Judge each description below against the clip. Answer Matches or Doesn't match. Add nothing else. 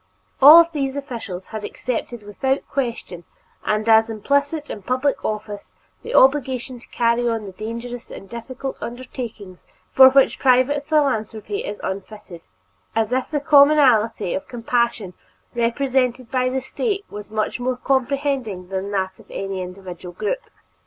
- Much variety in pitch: Doesn't match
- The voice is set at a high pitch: Matches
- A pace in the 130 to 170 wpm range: Matches